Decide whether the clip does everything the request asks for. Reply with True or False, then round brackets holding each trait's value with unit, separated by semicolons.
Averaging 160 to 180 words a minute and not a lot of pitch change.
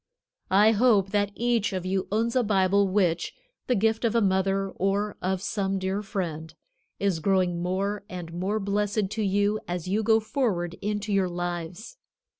True (170 wpm; 2.2 semitones)